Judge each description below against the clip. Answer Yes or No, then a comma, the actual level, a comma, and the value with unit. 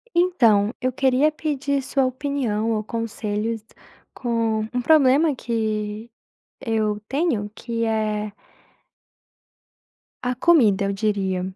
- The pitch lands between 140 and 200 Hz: No, high, 230 Hz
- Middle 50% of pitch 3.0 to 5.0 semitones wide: Yes, average, 4.0 semitones